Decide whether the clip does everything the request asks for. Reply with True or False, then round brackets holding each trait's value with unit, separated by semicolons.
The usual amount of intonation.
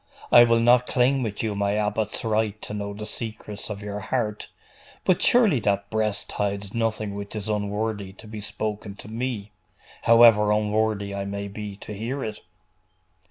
False (1.8 semitones)